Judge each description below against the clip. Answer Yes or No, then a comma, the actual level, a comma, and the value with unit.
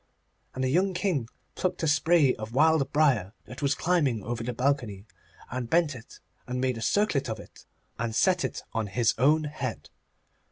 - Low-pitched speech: Yes, low, 130 Hz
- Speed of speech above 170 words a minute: Yes, average, 185 wpm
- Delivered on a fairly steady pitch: No, average, 5.2 semitones